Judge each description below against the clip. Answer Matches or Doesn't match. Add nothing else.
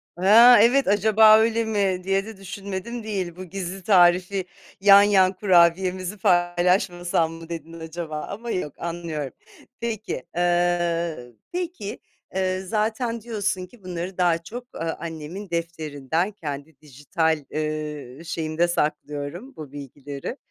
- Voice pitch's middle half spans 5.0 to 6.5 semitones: Doesn't match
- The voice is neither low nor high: Matches